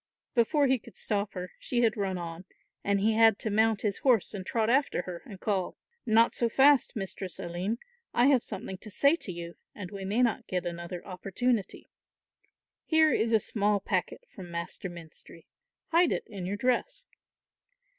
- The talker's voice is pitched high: Yes, high, 205 Hz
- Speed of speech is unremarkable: Yes, average, 180 wpm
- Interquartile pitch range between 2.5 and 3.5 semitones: No, average, 4.2 semitones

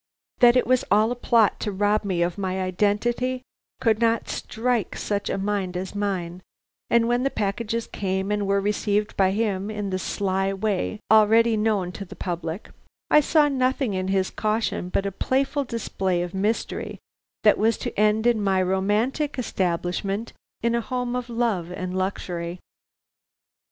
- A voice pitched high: Yes, high, 205 Hz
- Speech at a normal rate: Yes, average, 165 wpm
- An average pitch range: Yes, average, 3.5 semitones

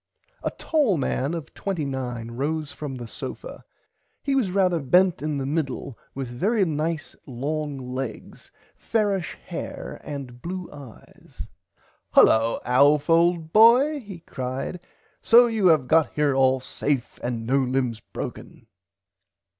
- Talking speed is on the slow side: Yes, slow, 130 wpm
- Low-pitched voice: No, medium, 150 Hz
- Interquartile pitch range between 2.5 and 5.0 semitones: No, wide, 5.6 semitones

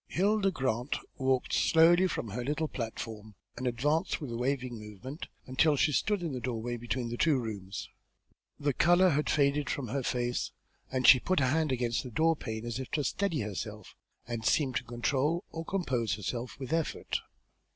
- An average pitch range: Yes, average, 4.6 semitones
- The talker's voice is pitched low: Yes, low, 130 Hz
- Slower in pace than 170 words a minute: No, average, 195 wpm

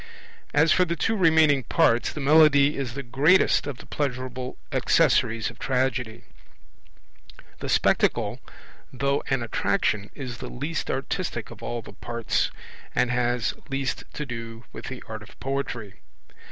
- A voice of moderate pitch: No, low, 130 Hz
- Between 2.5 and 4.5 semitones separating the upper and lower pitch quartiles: Yes, average, 3.3 semitones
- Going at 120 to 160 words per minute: Yes, average, 145 wpm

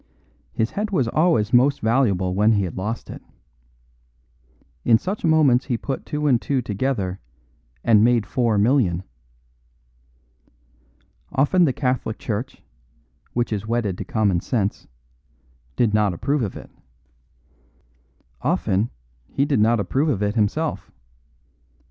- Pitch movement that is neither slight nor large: Yes, average, 4.7 semitones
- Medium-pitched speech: No, low, 115 Hz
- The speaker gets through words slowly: Yes, slow, 130 wpm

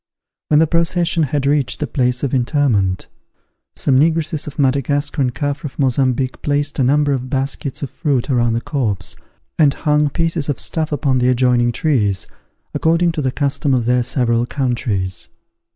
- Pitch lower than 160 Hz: Yes, medium, 140 Hz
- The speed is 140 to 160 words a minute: No, average, 170 wpm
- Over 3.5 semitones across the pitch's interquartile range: No, average, 3.1 semitones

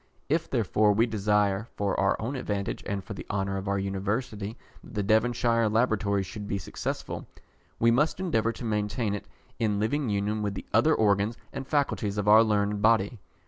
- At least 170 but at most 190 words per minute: Yes, average, 185 wpm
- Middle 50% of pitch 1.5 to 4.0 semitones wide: Yes, narrow, 2.4 semitones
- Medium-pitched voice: No, low, 105 Hz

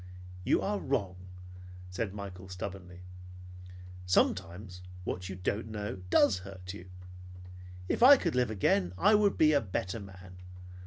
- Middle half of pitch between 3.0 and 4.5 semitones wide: Yes, average, 4.0 semitones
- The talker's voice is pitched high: No, very low, 95 Hz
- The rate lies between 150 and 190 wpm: No, average, 140 wpm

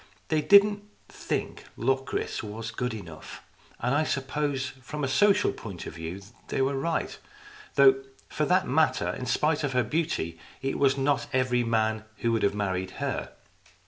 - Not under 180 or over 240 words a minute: No, average, 165 wpm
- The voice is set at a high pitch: No, low, 135 Hz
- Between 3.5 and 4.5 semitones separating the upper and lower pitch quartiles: No, average, 5.0 semitones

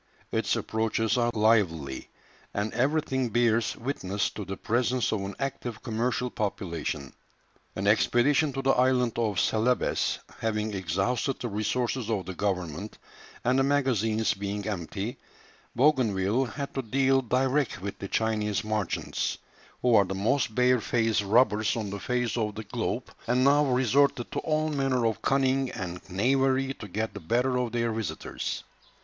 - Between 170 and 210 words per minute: No, average, 155 wpm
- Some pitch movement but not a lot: Yes, average, 3.8 semitones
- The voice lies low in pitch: Yes, low, 115 Hz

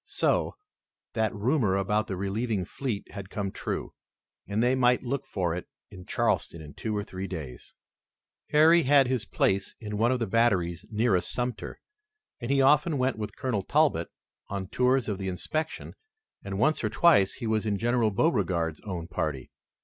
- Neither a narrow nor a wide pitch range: Yes, average, 4.8 semitones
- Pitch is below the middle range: Yes, low, 105 Hz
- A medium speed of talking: Yes, average, 170 wpm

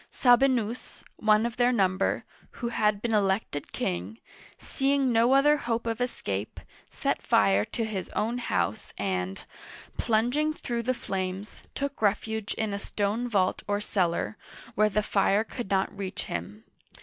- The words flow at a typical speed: Yes, average, 150 wpm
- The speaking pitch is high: Yes, high, 215 Hz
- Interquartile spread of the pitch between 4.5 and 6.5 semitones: No, average, 3.9 semitones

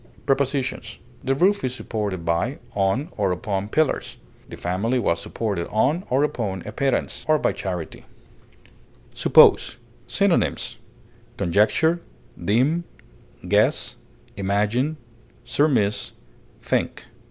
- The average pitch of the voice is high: No, low, 110 Hz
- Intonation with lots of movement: Yes, wide, 5.9 semitones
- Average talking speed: No, slow, 105 wpm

